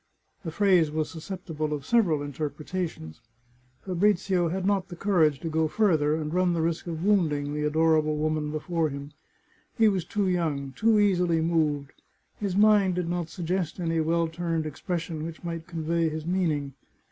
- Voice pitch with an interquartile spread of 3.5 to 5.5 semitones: No, average, 3.0 semitones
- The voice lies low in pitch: No, medium, 165 Hz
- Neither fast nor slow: Yes, average, 160 wpm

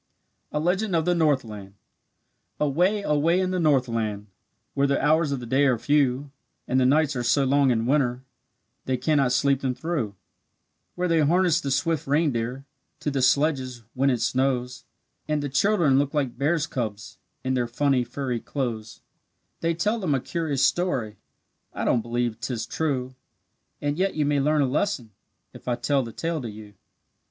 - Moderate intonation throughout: Yes, average, 3.9 semitones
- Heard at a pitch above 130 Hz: Yes, medium, 140 Hz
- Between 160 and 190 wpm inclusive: Yes, average, 175 wpm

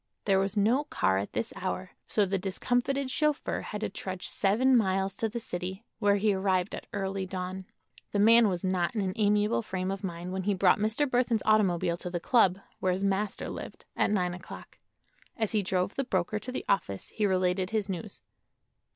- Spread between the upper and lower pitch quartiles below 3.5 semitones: Yes, average, 2.8 semitones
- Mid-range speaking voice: No, high, 195 Hz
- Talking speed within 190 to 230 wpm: Yes, average, 200 wpm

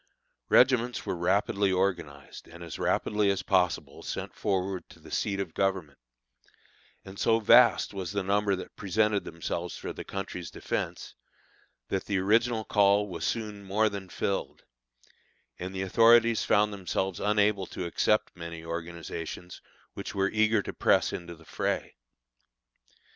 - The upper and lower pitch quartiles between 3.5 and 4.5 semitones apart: No, average, 2.8 semitones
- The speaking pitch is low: Yes, very low, 95 Hz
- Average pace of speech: Yes, average, 145 wpm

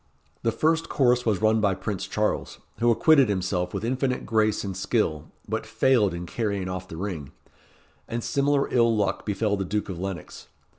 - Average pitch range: Yes, average, 4.1 semitones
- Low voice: Yes, low, 105 Hz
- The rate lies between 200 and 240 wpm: No, average, 180 wpm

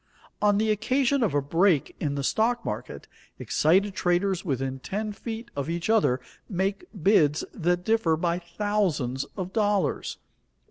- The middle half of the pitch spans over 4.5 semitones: Yes, average, 5.0 semitones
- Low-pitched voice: No, high, 190 Hz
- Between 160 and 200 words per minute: No, average, 145 wpm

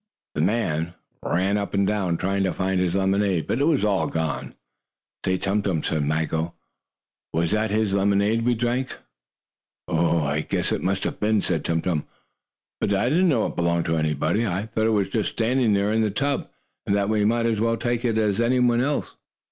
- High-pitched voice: No, low, 100 Hz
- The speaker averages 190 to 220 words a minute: Yes, fast, 205 wpm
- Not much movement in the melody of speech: No, average, 4.6 semitones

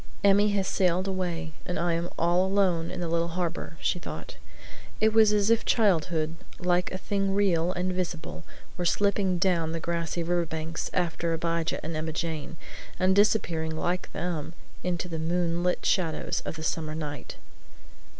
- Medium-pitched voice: Yes, medium, 175 Hz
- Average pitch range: No, narrow, 2.2 semitones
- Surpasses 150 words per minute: Yes, average, 170 wpm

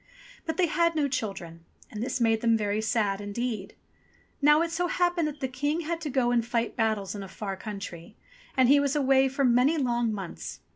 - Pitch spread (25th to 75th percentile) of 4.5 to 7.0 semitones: Yes, wide, 5.5 semitones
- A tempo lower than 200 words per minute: No, fast, 205 wpm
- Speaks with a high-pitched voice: Yes, high, 245 Hz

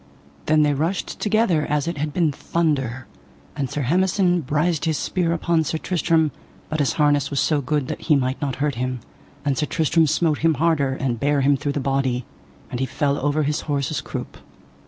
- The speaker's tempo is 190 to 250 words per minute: Yes, average, 200 wpm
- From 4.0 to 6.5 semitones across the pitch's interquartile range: No, average, 2.8 semitones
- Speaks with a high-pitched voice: No, medium, 150 Hz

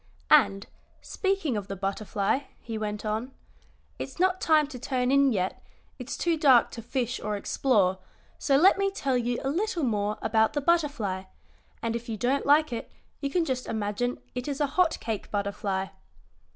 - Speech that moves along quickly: No, average, 180 wpm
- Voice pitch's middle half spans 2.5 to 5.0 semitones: No, wide, 5.5 semitones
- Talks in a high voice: Yes, very high, 250 Hz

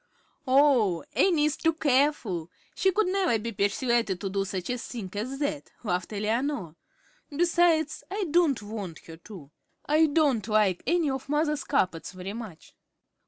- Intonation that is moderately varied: No, wide, 7.3 semitones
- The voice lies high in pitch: Yes, very high, 250 Hz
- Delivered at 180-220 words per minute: No, average, 155 wpm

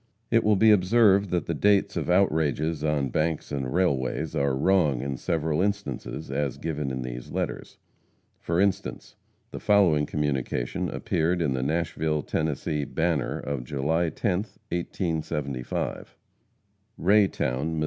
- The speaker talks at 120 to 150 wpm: Yes, average, 140 wpm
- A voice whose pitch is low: Yes, very low, 80 Hz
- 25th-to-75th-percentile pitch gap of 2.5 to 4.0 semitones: No, average, 4.7 semitones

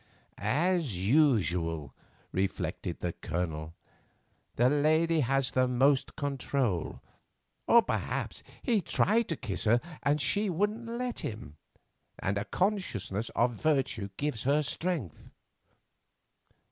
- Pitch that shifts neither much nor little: No, wide, 8.2 semitones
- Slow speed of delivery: Yes, slow, 110 wpm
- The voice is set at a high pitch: No, low, 135 Hz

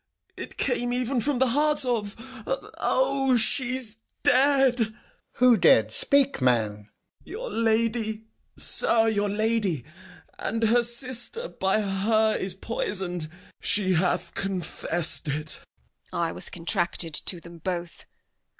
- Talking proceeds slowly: Yes, slow, 125 wpm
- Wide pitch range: Yes, wide, 5.7 semitones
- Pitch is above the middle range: Yes, high, 220 Hz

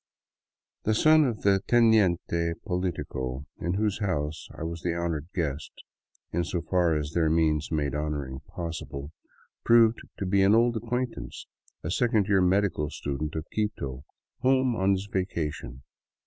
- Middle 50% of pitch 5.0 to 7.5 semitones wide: Yes, wide, 5.5 semitones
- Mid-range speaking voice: No, very low, 85 Hz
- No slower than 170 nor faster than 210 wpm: No, average, 155 wpm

